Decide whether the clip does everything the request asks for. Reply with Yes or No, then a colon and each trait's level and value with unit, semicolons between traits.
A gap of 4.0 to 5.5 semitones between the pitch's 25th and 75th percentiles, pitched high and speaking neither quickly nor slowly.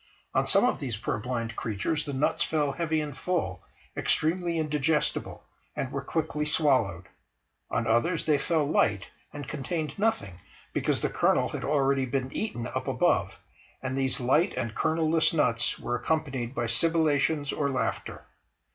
No: average, 4.5 semitones; medium, 140 Hz; average, 155 wpm